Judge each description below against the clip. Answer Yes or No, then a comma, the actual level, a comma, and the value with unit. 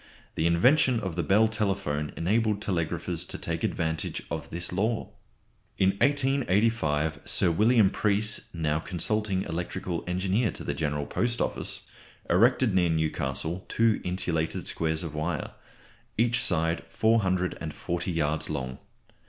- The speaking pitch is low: Yes, very low, 90 Hz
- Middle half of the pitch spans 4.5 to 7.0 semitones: Yes, average, 5.2 semitones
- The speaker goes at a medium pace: No, slow, 130 wpm